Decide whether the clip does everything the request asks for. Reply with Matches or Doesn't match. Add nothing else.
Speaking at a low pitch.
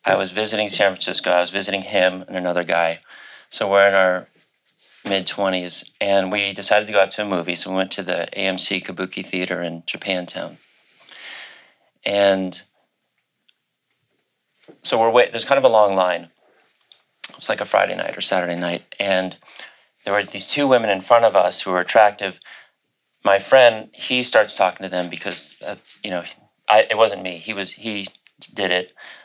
Matches